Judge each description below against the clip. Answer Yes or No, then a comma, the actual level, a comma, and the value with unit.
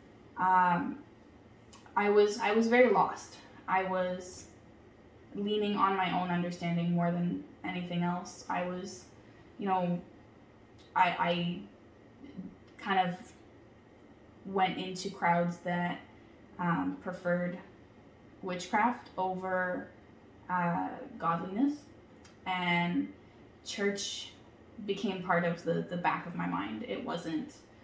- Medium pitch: Yes, medium, 180 Hz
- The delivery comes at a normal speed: No, slow, 105 wpm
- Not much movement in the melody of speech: Yes, narrow, 2.1 semitones